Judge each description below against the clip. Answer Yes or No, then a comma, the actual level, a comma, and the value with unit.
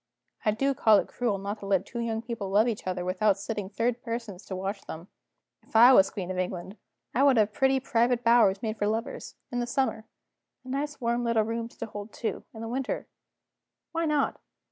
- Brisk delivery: Yes, fast, 210 wpm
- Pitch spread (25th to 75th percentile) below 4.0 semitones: Yes, average, 3.2 semitones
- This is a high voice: Yes, high, 225 Hz